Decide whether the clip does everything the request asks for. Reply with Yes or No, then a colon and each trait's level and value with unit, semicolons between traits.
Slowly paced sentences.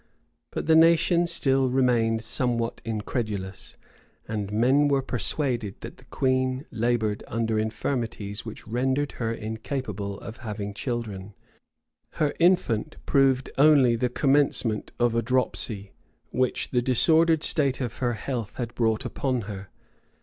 Yes: slow, 130 wpm